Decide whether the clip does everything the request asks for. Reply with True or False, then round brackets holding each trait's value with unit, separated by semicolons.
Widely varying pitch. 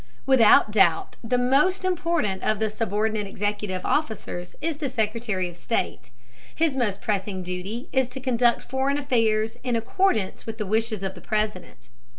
False (4.2 semitones)